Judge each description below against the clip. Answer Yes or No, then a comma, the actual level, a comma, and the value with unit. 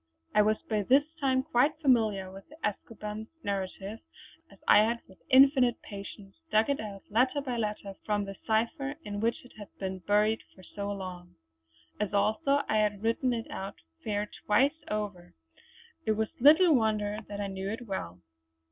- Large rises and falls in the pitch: No, average, 3.5 semitones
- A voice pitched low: No, high, 215 Hz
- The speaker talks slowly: No, average, 175 wpm